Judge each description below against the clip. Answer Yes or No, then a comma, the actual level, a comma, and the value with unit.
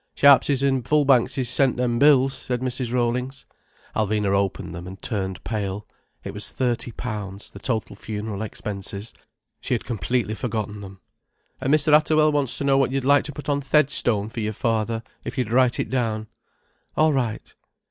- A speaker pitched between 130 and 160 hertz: No, low, 120 Hz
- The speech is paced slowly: No, average, 170 wpm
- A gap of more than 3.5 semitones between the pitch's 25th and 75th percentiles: Yes, average, 4.1 semitones